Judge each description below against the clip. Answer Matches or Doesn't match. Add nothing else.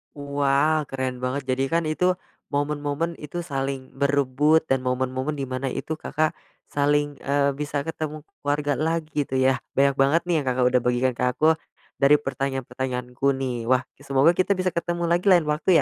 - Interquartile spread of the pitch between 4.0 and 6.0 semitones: Doesn't match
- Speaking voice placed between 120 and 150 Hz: Matches